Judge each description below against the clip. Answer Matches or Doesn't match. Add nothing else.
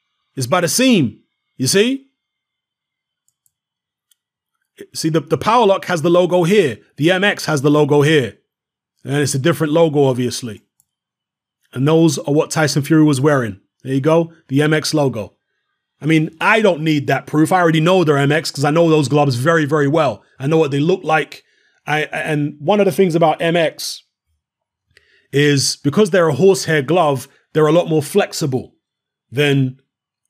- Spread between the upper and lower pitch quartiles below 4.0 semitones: Matches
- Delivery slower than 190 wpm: Matches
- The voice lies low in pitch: Doesn't match